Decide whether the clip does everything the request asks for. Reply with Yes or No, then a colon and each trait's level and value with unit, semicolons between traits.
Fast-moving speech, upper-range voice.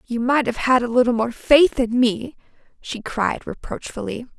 No: average, 180 wpm; high, 245 Hz